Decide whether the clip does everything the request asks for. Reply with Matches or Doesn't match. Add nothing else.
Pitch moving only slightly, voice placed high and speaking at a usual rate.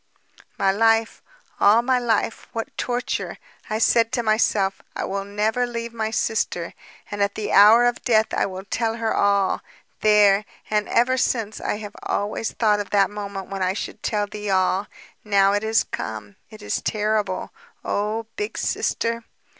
Matches